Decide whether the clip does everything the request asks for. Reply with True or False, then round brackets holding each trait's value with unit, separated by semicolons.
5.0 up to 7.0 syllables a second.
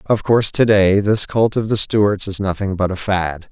False (4.7 syllables/s)